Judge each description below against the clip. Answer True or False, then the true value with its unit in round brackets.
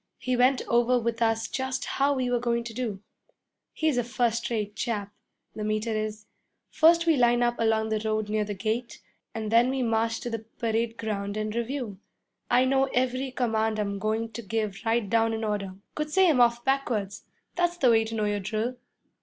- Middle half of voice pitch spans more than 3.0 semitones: False (2.5 semitones)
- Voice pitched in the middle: False (230 Hz)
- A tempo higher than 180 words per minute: True (200 wpm)